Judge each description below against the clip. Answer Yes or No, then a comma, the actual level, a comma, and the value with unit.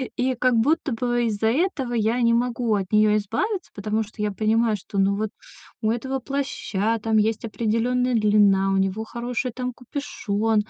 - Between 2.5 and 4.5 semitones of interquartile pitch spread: Yes, average, 2.8 semitones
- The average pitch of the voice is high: Yes, high, 225 Hz